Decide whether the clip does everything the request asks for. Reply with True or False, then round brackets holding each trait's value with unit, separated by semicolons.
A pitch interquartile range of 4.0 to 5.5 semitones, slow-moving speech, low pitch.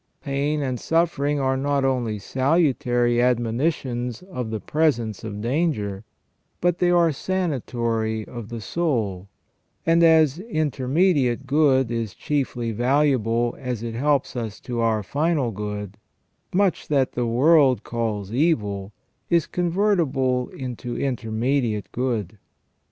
True (4.7 semitones; 125 wpm; 125 Hz)